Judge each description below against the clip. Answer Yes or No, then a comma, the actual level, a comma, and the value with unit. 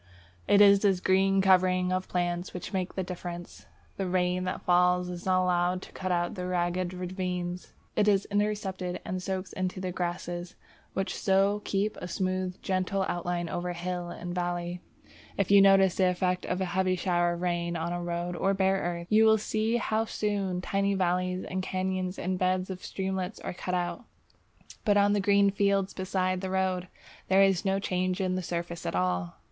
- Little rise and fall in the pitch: Yes, narrow, 1.4 semitones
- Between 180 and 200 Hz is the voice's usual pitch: Yes, medium, 185 Hz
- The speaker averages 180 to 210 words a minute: Yes, average, 185 wpm